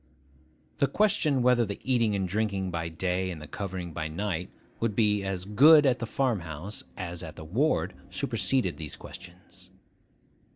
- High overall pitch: No, very low, 95 Hz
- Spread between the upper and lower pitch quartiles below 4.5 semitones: No, average, 4.9 semitones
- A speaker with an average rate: Yes, average, 165 wpm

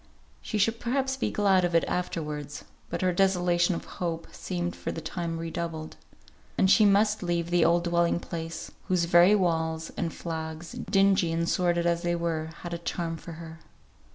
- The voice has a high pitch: No, medium, 170 Hz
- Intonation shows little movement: Yes, narrow, 1.9 semitones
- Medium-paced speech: Yes, average, 180 wpm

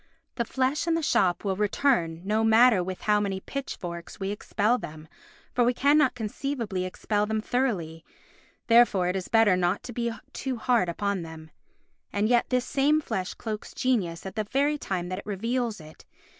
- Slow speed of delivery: No, average, 180 wpm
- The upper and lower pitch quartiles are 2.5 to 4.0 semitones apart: No, average, 5.2 semitones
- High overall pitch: Yes, high, 215 Hz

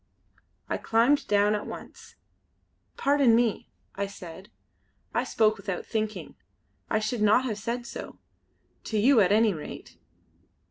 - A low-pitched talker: No, high, 215 Hz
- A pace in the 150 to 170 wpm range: No, slow, 135 wpm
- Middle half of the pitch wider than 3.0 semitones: No, narrow, 2.5 semitones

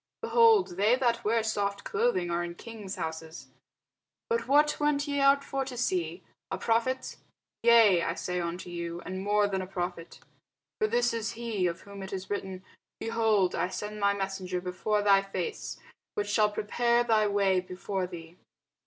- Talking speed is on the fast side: No, average, 170 wpm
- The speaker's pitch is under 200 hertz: No, high, 205 Hz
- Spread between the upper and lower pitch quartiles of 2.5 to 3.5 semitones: No, average, 4.2 semitones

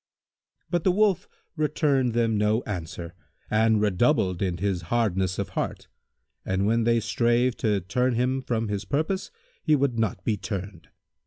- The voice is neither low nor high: No, low, 115 Hz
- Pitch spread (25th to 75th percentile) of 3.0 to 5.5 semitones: Yes, average, 4.5 semitones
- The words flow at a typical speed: Yes, average, 155 wpm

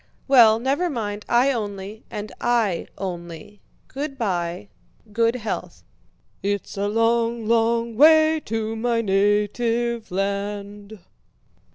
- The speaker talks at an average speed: No, slow, 105 wpm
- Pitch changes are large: No, narrow, 2.6 semitones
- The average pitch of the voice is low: No, high, 220 Hz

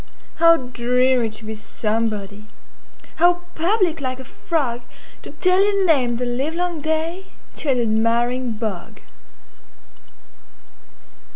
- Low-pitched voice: No, very high, 255 Hz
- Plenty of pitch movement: Yes, wide, 6.3 semitones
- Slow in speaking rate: Yes, slow, 95 wpm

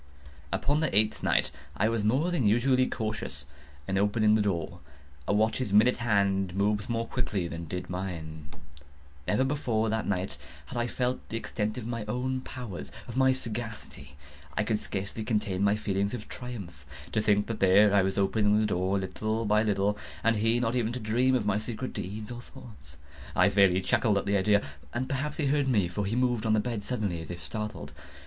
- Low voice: Yes, low, 105 Hz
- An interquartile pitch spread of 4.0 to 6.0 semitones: No, average, 3.5 semitones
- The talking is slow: No, average, 195 wpm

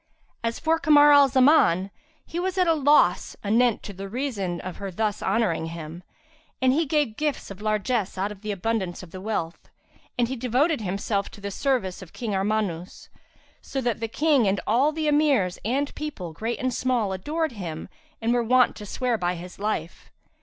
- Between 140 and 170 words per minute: No, average, 190 wpm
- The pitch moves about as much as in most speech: No, wide, 6.0 semitones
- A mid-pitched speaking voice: No, high, 225 Hz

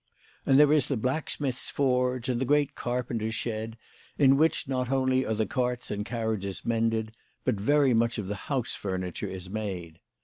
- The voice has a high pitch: No, low, 120 Hz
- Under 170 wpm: No, average, 175 wpm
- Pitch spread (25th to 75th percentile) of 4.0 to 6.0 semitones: No, average, 3.3 semitones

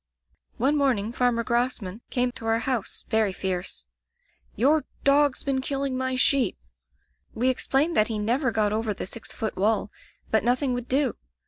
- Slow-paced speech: No, average, 160 wpm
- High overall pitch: Yes, high, 245 Hz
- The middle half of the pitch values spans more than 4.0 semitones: No, average, 3.4 semitones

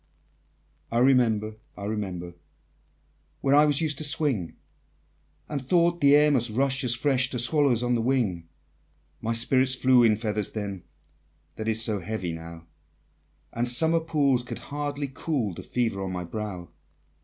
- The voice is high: No, low, 120 Hz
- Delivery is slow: No, average, 155 wpm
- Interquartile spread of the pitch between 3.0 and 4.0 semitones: No, average, 4.7 semitones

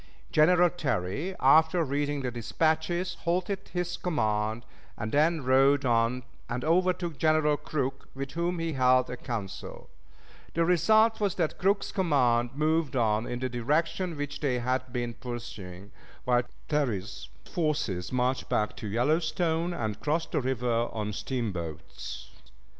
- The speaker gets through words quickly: No, average, 140 wpm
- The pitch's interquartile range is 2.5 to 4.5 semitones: No, wide, 5.6 semitones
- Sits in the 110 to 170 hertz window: Yes, medium, 140 Hz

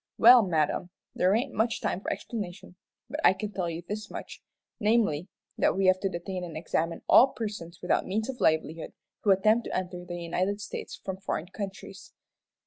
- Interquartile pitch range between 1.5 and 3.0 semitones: No, average, 3.4 semitones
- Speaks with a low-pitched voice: No, high, 190 Hz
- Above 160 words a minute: Yes, average, 185 wpm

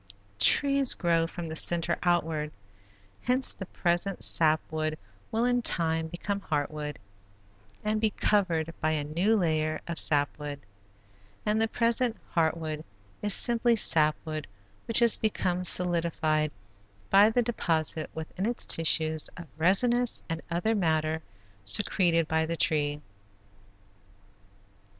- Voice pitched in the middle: Yes, medium, 170 Hz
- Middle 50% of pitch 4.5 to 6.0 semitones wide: Yes, average, 5.1 semitones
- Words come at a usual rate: No, slow, 130 wpm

